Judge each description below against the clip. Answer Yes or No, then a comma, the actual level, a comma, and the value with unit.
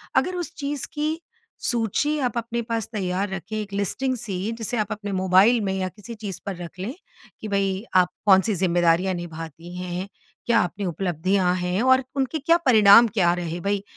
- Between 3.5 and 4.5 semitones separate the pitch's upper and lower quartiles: Yes, average, 4.2 semitones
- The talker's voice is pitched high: Yes, high, 200 Hz